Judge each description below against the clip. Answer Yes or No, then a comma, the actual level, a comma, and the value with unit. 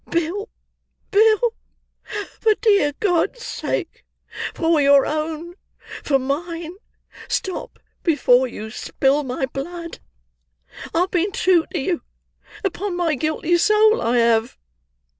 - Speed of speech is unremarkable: No, slow, 115 wpm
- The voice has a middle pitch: No, very high, 335 Hz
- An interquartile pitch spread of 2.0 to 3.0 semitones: No, average, 5.2 semitones